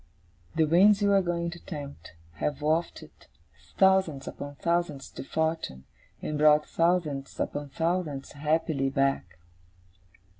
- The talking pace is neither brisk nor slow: No, slow, 120 wpm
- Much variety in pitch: No, average, 3.3 semitones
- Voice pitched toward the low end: No, medium, 155 Hz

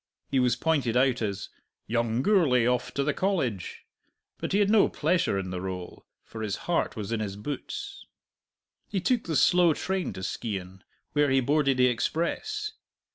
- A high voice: No, low, 130 Hz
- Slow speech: No, average, 175 wpm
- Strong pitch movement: Yes, wide, 8.0 semitones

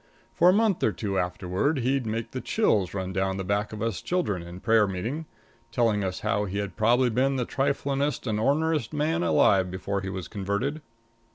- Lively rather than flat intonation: Yes, wide, 6.1 semitones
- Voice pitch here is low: Yes, low, 110 Hz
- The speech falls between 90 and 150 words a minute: No, average, 190 wpm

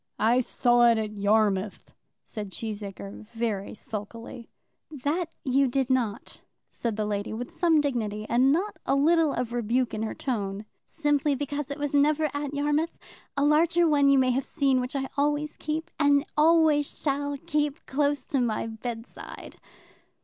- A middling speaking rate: Yes, average, 160 wpm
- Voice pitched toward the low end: No, very high, 270 Hz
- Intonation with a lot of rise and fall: No, average, 4.6 semitones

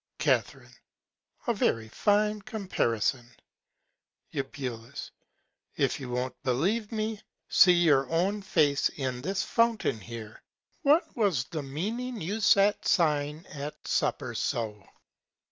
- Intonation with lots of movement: Yes, wide, 8.2 semitones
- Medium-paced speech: No, slow, 110 wpm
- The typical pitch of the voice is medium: Yes, medium, 155 Hz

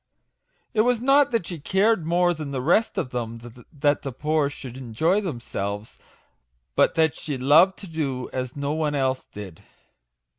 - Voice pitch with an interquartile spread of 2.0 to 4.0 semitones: No, wide, 5.4 semitones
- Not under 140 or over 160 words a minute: No, average, 175 wpm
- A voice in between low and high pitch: Yes, medium, 150 Hz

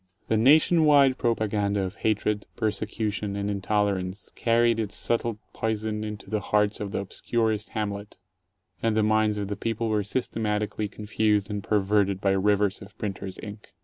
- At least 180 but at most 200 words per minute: No, average, 155 wpm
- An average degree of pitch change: No, narrow, 1.4 semitones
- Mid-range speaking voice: No, low, 105 Hz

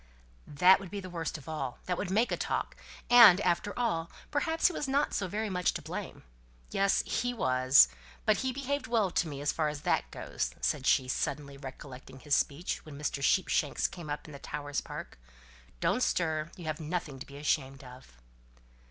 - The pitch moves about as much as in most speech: No, wide, 5.9 semitones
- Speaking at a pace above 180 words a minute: Yes, average, 200 wpm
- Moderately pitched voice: Yes, medium, 160 Hz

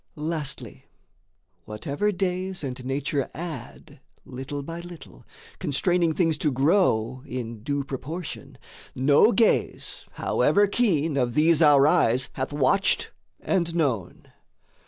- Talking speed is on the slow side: Yes, slow, 115 wpm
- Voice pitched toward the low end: No, medium, 150 Hz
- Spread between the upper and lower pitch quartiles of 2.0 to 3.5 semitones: No, average, 4.7 semitones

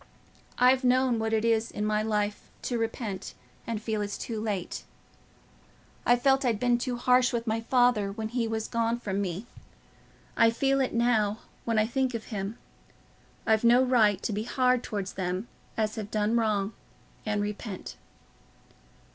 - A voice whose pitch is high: Yes, high, 225 Hz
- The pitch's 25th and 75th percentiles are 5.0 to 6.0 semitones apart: No, narrow, 2.5 semitones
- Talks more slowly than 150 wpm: No, average, 165 wpm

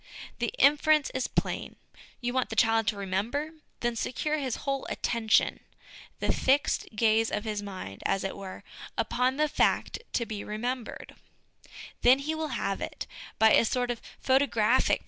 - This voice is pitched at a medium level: No, high, 240 Hz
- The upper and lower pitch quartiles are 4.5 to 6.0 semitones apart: No, average, 4.0 semitones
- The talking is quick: No, average, 160 wpm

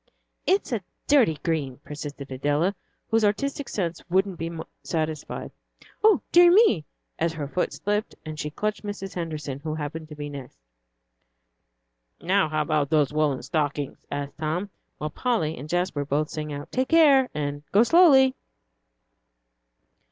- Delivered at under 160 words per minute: Yes, average, 145 wpm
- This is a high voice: No, medium, 160 Hz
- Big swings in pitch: Yes, wide, 5.9 semitones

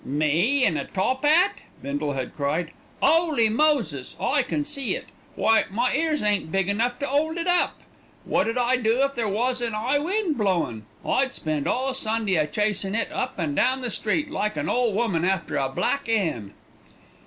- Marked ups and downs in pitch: Yes, wide, 7.9 semitones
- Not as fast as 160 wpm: No, average, 190 wpm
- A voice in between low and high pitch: No, high, 225 Hz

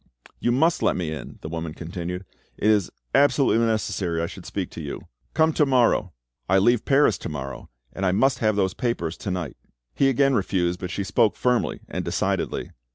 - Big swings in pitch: Yes, wide, 5.9 semitones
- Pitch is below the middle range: Yes, low, 100 Hz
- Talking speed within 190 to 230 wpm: Yes, average, 195 wpm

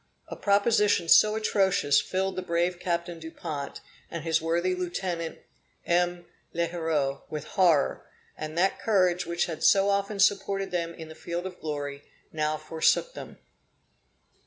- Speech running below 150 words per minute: Yes, average, 140 wpm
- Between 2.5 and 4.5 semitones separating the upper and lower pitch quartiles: Yes, average, 2.9 semitones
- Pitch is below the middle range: No, medium, 175 Hz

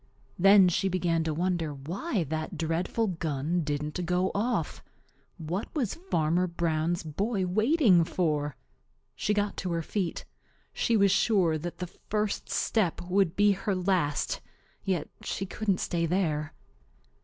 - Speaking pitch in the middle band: Yes, medium, 180 Hz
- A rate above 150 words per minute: No, average, 140 wpm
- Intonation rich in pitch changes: No, average, 3.6 semitones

